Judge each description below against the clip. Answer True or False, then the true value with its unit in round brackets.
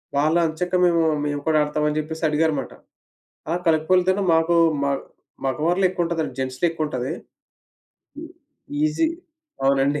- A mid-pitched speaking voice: True (155 Hz)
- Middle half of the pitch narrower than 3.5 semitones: True (2.5 semitones)